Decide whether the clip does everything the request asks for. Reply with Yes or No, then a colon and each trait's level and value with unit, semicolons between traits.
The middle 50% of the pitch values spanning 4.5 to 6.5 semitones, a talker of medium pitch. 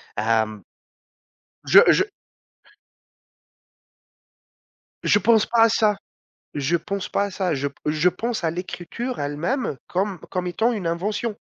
Yes: wide, 5.6 semitones; medium, 180 Hz